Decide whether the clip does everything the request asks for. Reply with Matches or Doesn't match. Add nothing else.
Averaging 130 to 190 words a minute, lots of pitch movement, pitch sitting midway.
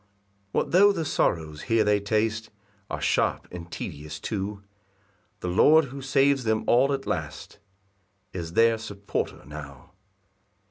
Doesn't match